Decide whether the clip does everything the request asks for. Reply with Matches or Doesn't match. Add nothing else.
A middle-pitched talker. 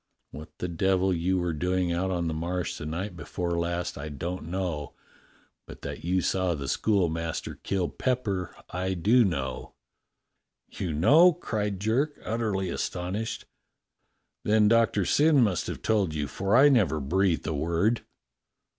Doesn't match